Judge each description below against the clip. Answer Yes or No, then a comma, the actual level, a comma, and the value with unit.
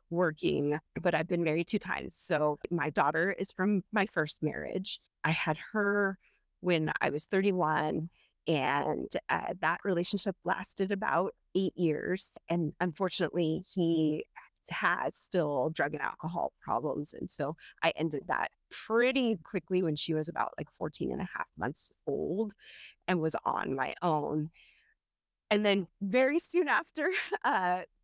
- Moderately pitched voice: Yes, medium, 180 Hz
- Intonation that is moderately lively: Yes, average, 3.7 semitones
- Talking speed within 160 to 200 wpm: No, average, 145 wpm